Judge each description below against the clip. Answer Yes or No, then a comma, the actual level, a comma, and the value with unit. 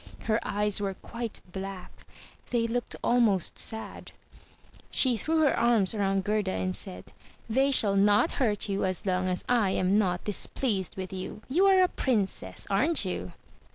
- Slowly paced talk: No, average, 160 wpm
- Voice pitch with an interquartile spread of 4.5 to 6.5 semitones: No, average, 3.9 semitones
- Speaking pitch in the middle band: No, high, 205 Hz